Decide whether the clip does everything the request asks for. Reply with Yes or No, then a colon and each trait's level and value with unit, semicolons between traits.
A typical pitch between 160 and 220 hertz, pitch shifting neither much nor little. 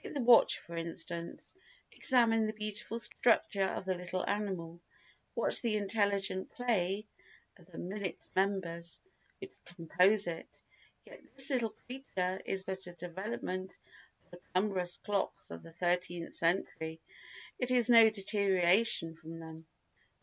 Yes: high, 190 Hz; average, 3.7 semitones